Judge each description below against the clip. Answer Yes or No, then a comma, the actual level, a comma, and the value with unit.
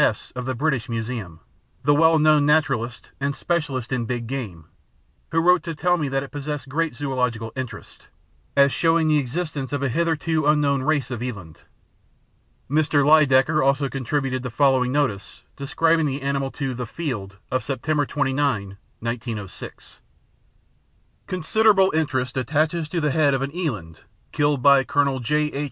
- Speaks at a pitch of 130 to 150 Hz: Yes, medium, 140 Hz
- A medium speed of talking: Yes, average, 155 wpm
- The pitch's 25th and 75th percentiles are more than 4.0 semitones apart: No, average, 3.4 semitones